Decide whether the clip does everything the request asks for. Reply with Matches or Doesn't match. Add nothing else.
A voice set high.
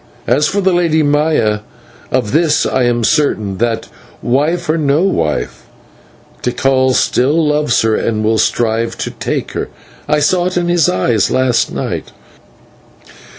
Doesn't match